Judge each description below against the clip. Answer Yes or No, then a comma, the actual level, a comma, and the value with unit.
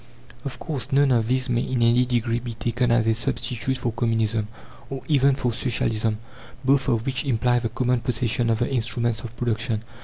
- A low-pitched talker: Yes, low, 120 Hz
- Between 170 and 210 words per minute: Yes, average, 190 wpm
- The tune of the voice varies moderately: No, narrow, 2.1 semitones